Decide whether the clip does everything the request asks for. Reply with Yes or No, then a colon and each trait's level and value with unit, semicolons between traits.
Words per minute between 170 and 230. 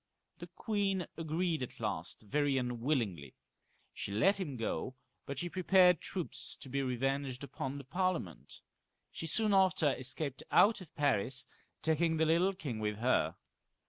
No: average, 145 wpm